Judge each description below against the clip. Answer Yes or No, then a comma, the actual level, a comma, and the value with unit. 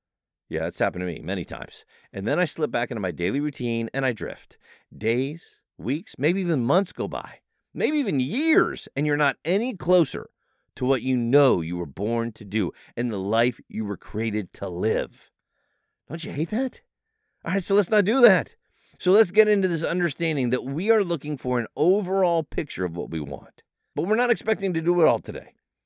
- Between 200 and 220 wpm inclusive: Yes, fast, 205 wpm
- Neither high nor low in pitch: Yes, medium, 145 Hz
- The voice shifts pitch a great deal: Yes, wide, 8.8 semitones